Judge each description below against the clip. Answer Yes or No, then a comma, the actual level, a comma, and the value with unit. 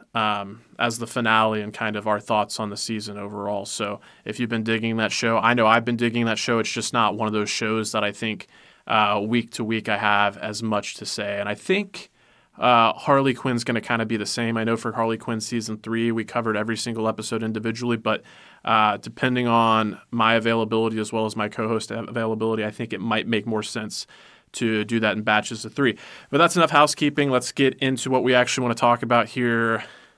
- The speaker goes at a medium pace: No, fast, 230 wpm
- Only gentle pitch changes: Yes, narrow, 1.7 semitones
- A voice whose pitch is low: Yes, low, 115 Hz